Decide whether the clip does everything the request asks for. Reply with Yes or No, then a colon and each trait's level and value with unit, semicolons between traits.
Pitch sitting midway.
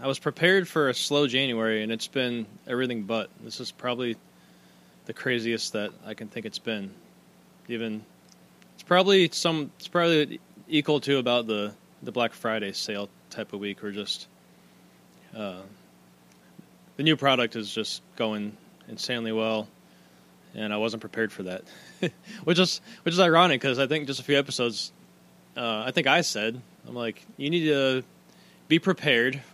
No: low, 115 Hz